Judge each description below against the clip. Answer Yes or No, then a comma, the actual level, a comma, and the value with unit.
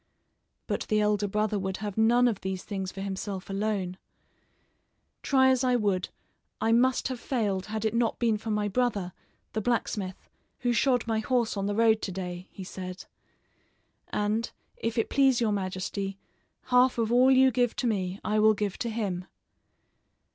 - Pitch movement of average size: Yes, average, 3.5 semitones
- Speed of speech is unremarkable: Yes, average, 175 wpm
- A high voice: Yes, high, 215 Hz